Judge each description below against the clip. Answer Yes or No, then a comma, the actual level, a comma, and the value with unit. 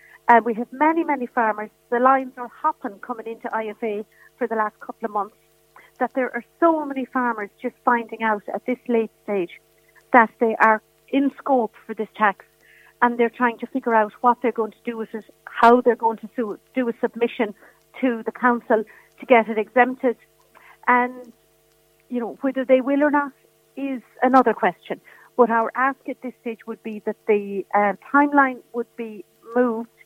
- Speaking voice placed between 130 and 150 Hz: No, high, 240 Hz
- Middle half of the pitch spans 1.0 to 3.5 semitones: Yes, narrow, 2.4 semitones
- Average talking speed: Yes, average, 190 wpm